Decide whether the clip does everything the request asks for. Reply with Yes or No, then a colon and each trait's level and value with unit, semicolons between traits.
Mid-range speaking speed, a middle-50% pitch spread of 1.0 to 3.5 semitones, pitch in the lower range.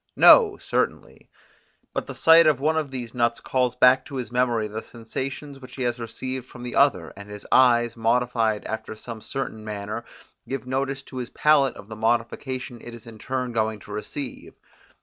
Yes: average, 190 wpm; average, 2.9 semitones; low, 125 Hz